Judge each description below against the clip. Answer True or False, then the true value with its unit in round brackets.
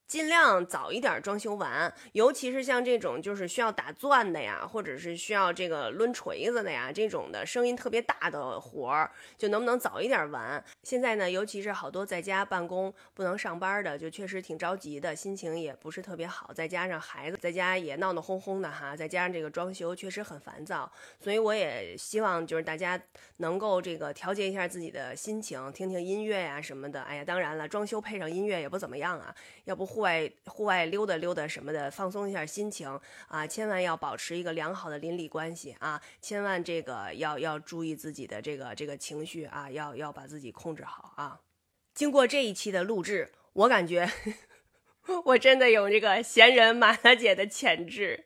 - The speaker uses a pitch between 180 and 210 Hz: True (185 Hz)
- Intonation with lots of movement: False (4.8 semitones)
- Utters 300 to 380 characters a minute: True (310 characters per minute)